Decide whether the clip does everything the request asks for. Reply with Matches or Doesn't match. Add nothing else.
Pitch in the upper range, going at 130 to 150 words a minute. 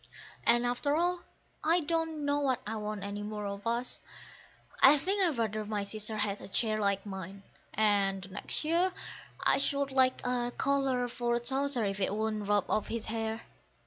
Doesn't match